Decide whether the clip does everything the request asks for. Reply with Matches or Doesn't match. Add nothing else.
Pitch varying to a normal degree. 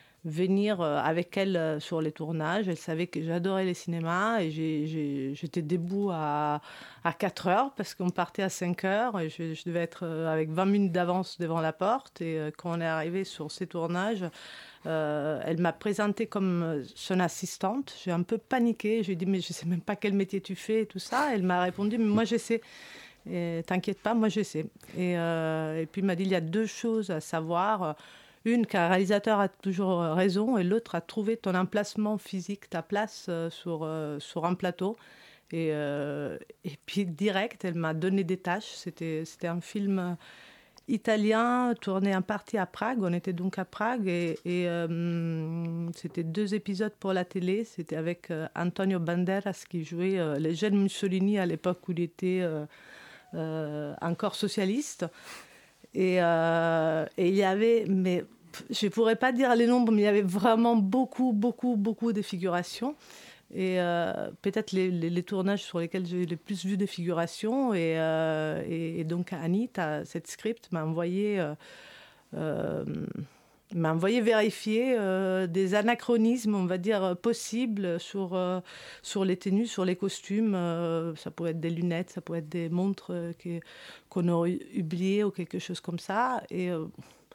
Matches